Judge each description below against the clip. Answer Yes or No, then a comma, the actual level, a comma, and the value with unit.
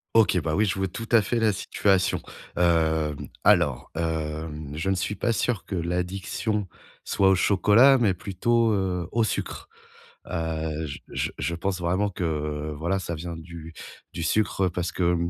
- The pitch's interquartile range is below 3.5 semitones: No, average, 3.8 semitones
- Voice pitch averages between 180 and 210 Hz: No, very low, 90 Hz